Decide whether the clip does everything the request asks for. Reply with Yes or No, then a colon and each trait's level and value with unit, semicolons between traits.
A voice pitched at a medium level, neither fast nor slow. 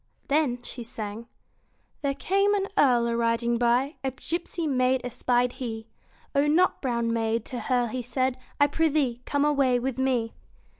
No: very high, 255 Hz; average, 160 wpm